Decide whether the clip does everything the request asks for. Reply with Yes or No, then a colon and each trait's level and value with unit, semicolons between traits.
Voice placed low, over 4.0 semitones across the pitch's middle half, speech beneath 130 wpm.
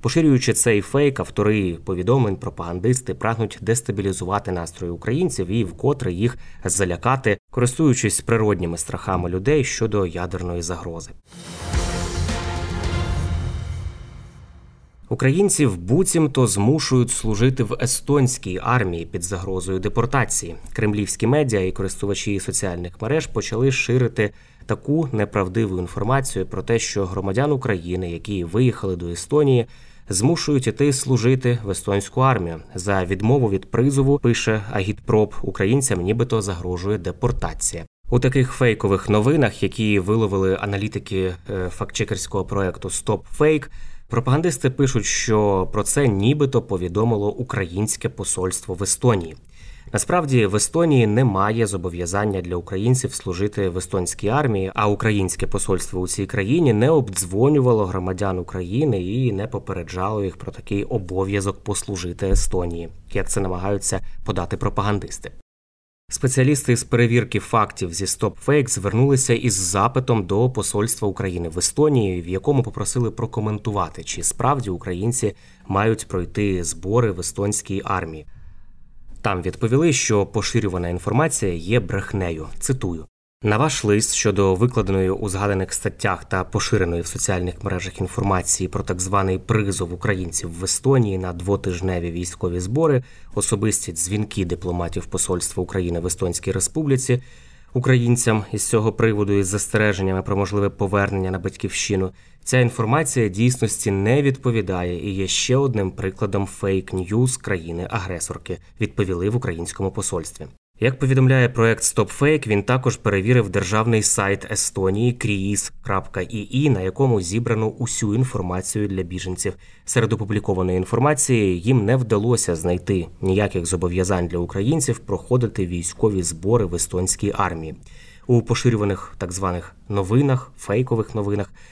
Yes: low, 105 Hz; average, 4.4 semitones; average, 120 wpm